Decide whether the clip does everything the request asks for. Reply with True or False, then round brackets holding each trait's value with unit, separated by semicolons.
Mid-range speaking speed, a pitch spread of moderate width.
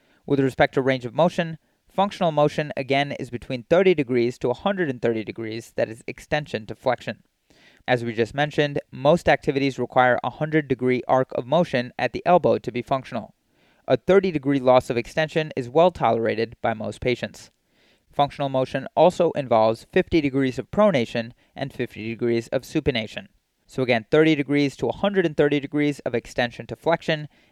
True (165 wpm; 4.2 semitones)